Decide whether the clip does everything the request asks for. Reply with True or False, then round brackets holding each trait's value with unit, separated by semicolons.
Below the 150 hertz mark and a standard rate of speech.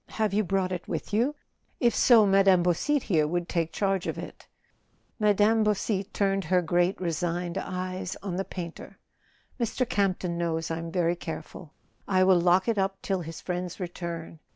False (185 Hz; 175 wpm)